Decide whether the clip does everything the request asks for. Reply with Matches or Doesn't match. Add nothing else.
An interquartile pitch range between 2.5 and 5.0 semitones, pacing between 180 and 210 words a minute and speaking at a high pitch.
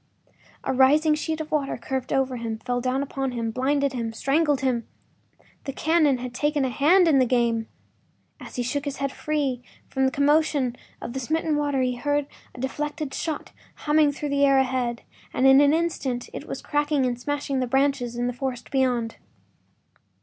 Matches